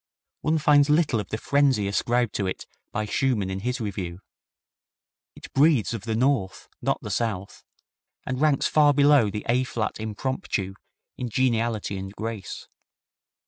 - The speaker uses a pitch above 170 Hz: No, low, 115 Hz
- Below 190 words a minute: Yes, average, 150 wpm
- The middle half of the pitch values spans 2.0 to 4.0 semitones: No, average, 4.8 semitones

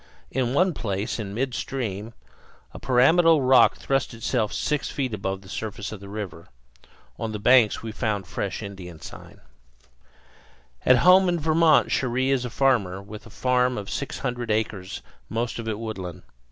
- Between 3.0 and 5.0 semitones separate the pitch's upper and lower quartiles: Yes, average, 4.3 semitones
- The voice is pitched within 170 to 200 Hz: No, low, 115 Hz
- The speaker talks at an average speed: Yes, average, 165 wpm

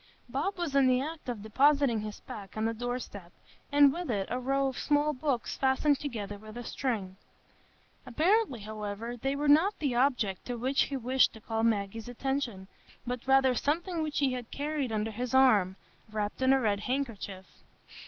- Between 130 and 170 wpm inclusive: No, average, 185 wpm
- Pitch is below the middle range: No, very high, 250 Hz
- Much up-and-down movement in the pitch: No, average, 4.3 semitones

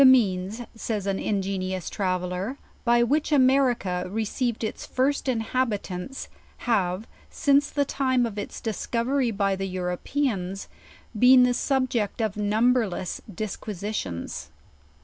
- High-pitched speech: Yes, high, 220 Hz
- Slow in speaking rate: Yes, slow, 125 wpm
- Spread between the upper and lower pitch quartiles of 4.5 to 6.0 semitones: Yes, average, 4.8 semitones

